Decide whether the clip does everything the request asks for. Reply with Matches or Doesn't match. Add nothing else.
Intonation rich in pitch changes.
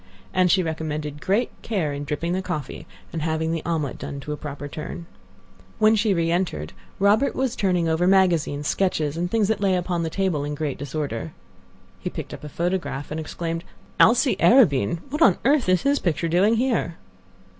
Doesn't match